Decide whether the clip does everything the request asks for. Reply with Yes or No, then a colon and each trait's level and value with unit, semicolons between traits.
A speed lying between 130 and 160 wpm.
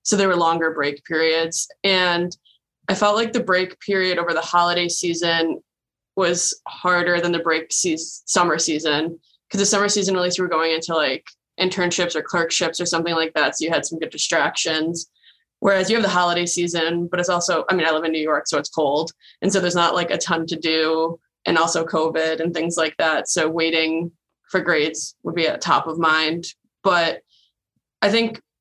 No: fast, 205 wpm